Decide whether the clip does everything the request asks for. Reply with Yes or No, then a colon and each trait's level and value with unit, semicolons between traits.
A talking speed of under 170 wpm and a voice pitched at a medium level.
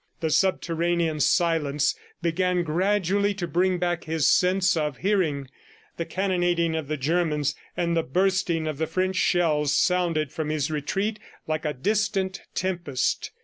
Yes: average, 145 wpm; medium, 170 Hz